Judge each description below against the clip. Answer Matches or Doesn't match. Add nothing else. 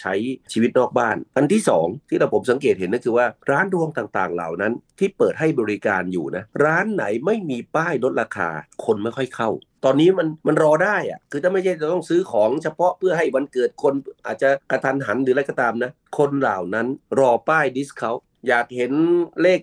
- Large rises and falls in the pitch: Matches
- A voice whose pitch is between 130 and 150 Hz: Matches